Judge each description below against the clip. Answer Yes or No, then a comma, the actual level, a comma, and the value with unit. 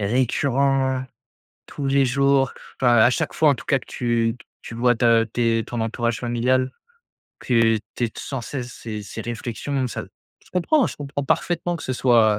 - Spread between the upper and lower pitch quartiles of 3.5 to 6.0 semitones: No, average, 2.9 semitones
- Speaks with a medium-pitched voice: No, low, 125 Hz